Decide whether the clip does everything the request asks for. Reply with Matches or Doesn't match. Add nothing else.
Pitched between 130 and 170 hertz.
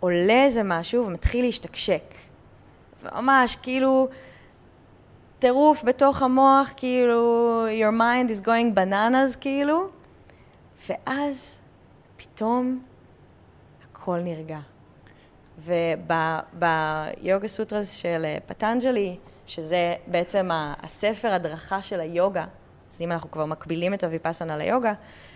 Doesn't match